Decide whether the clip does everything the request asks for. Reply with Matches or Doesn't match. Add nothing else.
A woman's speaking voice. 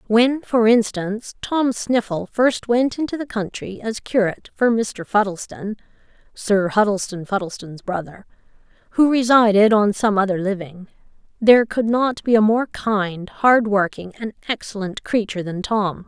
Matches